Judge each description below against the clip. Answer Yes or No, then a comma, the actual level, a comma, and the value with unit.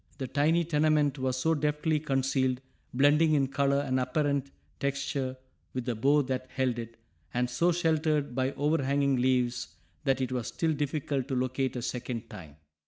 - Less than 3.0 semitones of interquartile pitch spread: Yes, narrow, 2.5 semitones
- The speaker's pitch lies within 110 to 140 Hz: Yes, low, 135 Hz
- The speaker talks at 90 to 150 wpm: No, average, 165 wpm